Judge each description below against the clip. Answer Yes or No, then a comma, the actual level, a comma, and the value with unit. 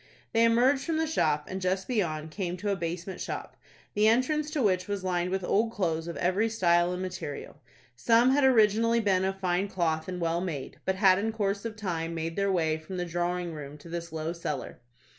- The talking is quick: Yes, fast, 215 wpm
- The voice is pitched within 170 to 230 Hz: Yes, medium, 185 Hz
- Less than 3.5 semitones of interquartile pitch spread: No, average, 4.1 semitones